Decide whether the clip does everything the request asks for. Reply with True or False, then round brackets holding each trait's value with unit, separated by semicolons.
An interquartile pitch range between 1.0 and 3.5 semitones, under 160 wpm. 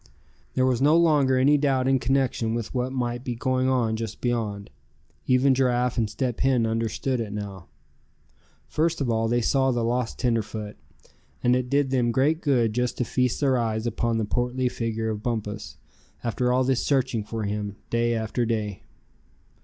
False (2.6 semitones; 175 wpm)